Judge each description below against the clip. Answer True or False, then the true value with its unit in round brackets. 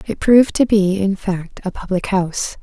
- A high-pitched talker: True (195 Hz)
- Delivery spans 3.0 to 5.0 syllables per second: True (4.9 syllables/s)